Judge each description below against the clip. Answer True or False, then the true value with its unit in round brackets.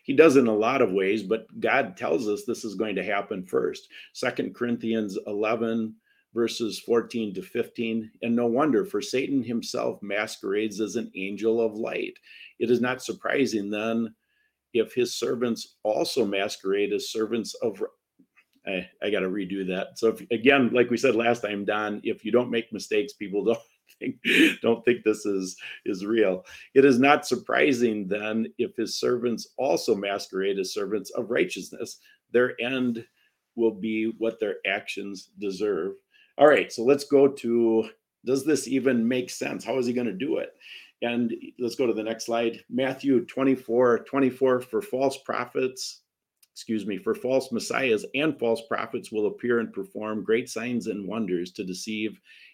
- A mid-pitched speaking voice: False (120 Hz)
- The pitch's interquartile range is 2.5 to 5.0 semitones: True (3.7 semitones)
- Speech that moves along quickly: False (170 wpm)